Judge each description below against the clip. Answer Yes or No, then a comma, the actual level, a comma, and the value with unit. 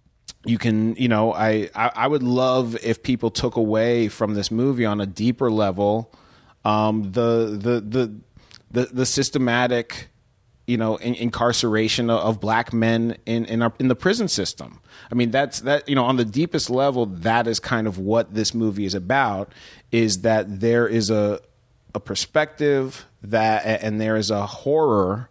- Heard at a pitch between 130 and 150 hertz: No, low, 115 Hz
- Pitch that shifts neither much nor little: No, narrow, 2.1 semitones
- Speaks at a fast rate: No, average, 175 wpm